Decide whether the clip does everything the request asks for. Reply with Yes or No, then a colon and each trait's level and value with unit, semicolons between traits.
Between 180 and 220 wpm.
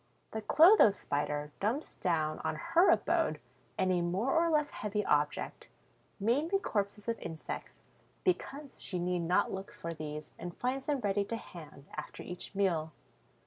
No: average, 150 wpm